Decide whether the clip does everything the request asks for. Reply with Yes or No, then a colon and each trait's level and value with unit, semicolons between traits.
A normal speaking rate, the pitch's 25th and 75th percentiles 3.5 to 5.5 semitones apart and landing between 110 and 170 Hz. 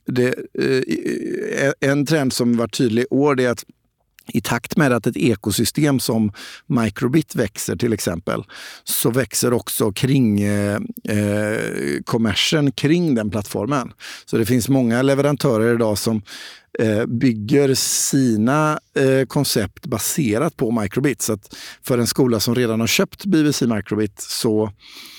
Yes: average, 140 wpm; average, 4.0 semitones; low, 120 Hz